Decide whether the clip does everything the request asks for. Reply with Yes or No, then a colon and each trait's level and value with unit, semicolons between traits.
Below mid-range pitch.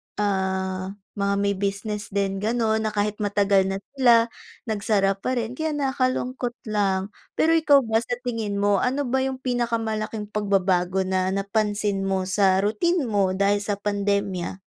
No: high, 205 Hz